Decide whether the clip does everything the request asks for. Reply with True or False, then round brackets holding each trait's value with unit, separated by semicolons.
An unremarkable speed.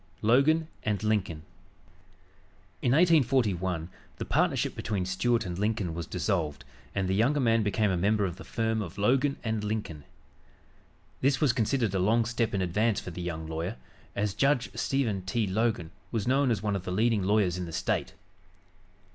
True (170 wpm)